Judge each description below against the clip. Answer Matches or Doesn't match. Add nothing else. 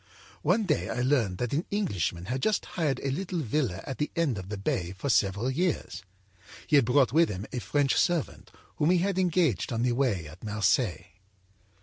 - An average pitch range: Doesn't match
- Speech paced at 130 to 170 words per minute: Doesn't match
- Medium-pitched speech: Doesn't match